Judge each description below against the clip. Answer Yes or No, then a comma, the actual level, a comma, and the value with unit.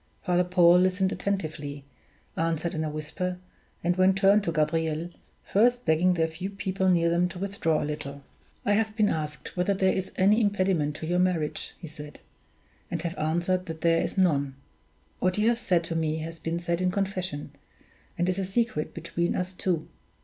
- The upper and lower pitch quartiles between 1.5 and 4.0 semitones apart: Yes, average, 2.9 semitones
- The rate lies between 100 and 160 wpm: No, average, 185 wpm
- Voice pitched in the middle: Yes, medium, 175 Hz